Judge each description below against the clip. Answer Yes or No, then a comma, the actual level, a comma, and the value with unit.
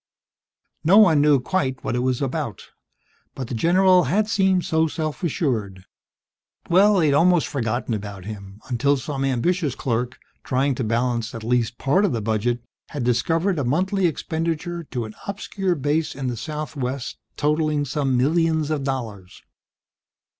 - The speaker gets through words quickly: No, average, 155 wpm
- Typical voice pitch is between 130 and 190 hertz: Yes, medium, 140 Hz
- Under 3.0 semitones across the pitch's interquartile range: No, average, 5.3 semitones